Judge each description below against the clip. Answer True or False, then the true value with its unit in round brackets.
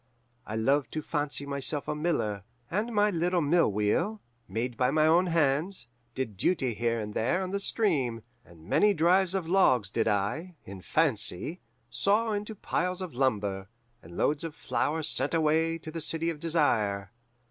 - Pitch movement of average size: False (7.2 semitones)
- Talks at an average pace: True (170 wpm)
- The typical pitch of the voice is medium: True (150 Hz)